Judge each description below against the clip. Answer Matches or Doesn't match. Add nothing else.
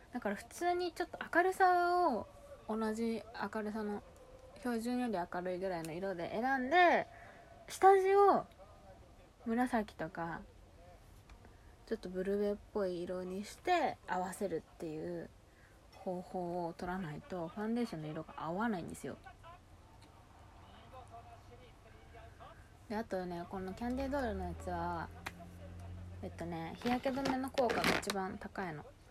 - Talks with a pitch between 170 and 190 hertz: Matches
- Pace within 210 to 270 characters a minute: Matches